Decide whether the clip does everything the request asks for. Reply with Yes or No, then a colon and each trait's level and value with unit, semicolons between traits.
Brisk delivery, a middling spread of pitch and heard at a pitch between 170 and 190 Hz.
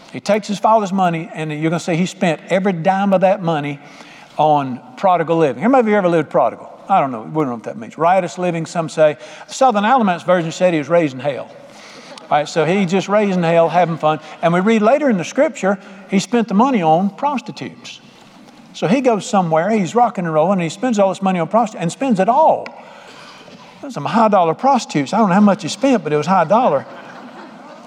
Yes: fast, 225 wpm; average, 4.5 semitones; medium, 185 Hz